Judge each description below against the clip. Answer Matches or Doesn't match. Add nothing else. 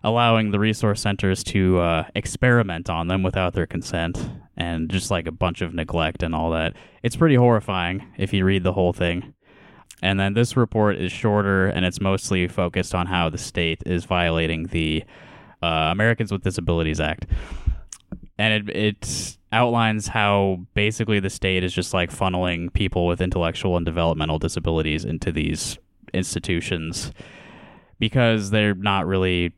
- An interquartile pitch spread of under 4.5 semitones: Matches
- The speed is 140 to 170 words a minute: Matches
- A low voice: Matches